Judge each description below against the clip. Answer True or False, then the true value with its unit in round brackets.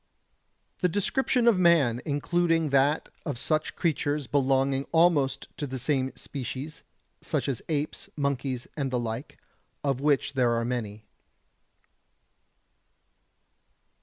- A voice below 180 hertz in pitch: True (140 Hz)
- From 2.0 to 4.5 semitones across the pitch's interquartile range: True (3.1 semitones)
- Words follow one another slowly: True (115 wpm)